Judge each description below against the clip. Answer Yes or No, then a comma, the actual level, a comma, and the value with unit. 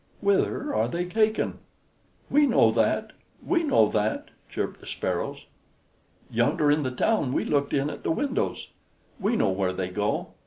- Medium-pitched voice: Yes, medium, 150 Hz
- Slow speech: No, average, 160 wpm